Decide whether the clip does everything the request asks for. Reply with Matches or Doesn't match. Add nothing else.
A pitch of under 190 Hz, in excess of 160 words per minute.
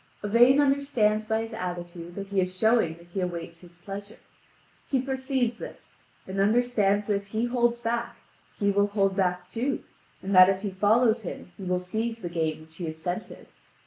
Doesn't match